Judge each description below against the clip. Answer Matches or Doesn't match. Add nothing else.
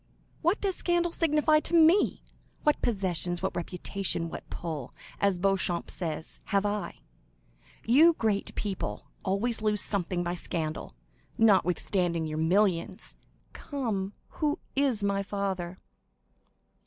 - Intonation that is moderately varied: Doesn't match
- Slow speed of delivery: Matches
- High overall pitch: Matches